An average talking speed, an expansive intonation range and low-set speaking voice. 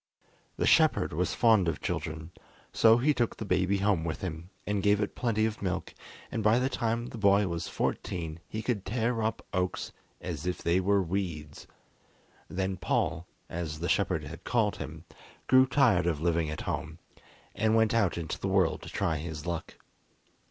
No: average, 180 wpm; average, 4.9 semitones; very low, 95 Hz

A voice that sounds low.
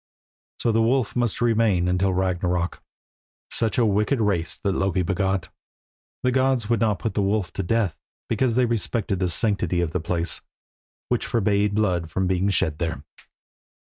Yes: low, 100 Hz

